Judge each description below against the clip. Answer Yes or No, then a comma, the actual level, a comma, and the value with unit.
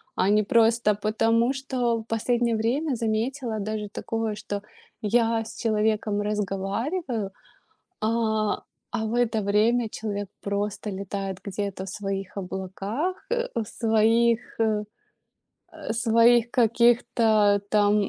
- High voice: Yes, high, 220 Hz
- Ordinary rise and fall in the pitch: No, narrow, 2.2 semitones